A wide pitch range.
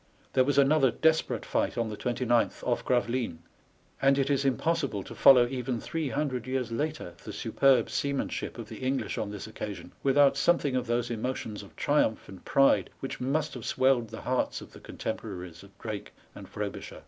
No: average, 3.5 semitones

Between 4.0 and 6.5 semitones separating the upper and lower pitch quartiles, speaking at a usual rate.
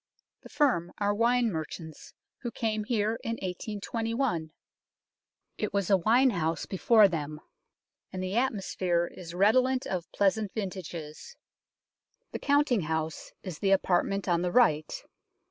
No: average, 5.0 semitones; slow, 130 wpm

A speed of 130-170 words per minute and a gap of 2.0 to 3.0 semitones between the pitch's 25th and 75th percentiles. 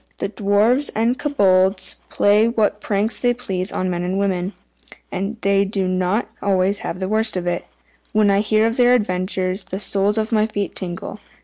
No: average, 185 wpm; average, 2.7 semitones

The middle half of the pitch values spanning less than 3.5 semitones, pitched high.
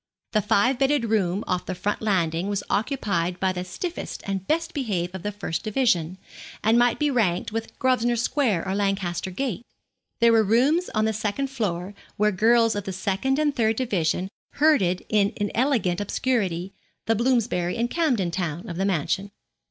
No: average, 4.6 semitones; high, 210 Hz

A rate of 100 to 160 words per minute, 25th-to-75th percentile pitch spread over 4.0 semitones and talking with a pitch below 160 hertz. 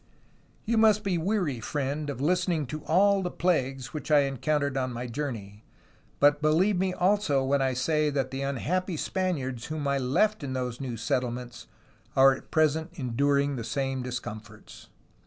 No: average, 170 wpm; average, 4.4 semitones; medium, 140 Hz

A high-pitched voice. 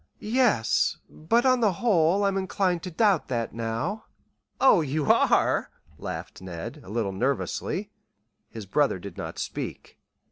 No: medium, 160 Hz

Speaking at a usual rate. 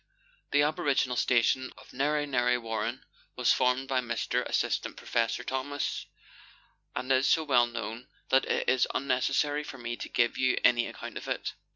Yes: average, 165 wpm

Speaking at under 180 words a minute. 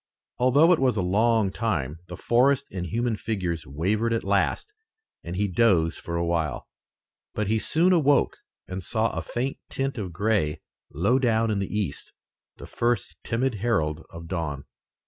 Yes: average, 165 wpm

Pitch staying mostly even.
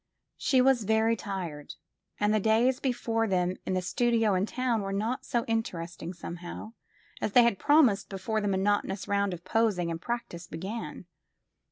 No: average, 3.8 semitones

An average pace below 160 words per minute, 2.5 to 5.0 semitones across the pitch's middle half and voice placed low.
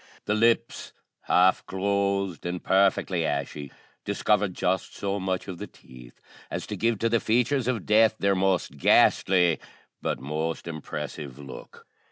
Yes: average, 145 wpm; average, 4.4 semitones; very low, 95 Hz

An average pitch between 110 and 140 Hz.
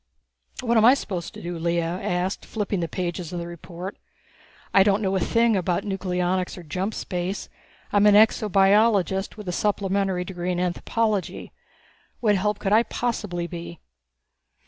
No: high, 190 Hz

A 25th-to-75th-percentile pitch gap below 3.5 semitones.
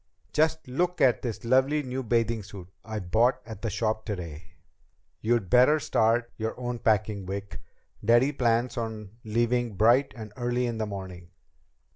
Yes: average, 2.7 semitones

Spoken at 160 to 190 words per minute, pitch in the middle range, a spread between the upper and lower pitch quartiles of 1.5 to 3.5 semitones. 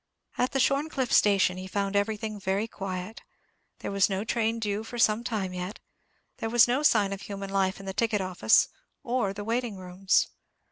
No: average, 185 wpm; high, 205 Hz; average, 2.9 semitones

